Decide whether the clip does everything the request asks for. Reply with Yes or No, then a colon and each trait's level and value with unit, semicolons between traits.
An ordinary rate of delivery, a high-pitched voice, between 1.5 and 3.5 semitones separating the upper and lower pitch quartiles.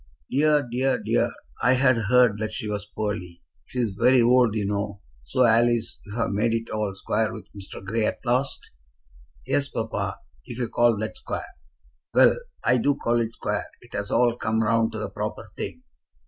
No: average, 185 wpm; low, 115 Hz; average, 2.8 semitones